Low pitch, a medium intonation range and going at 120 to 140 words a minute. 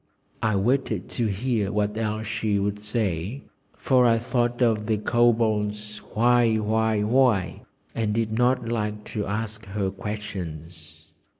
No: low, 110 Hz; narrow, 2.0 semitones; slow, 135 wpm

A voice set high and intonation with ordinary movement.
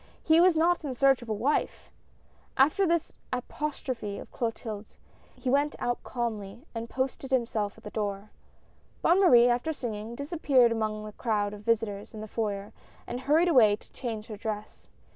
Yes: high, 235 Hz; average, 4.5 semitones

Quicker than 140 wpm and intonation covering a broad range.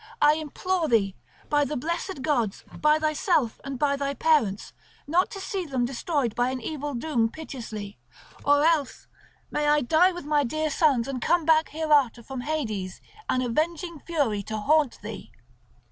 No: average, 165 wpm; average, 4.3 semitones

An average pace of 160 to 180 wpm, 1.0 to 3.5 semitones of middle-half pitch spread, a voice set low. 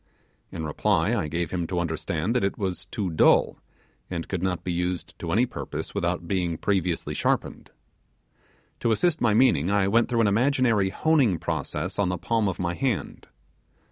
No: average, 175 wpm; average, 4.6 semitones; very low, 95 Hz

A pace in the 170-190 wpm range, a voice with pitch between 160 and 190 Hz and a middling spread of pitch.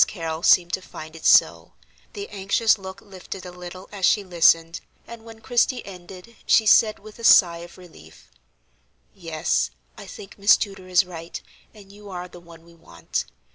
Yes: average, 175 wpm; medium, 185 Hz; average, 3.2 semitones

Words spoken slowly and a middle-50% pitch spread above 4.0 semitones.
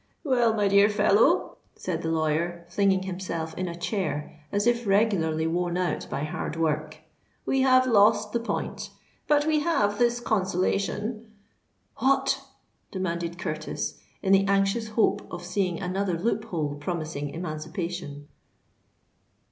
Yes: slow, 130 wpm; average, 4.5 semitones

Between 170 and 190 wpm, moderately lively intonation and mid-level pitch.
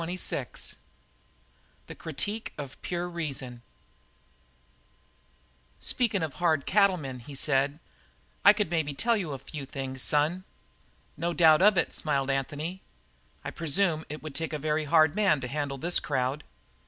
No: average, 145 wpm; average, 4.1 semitones; medium, 155 Hz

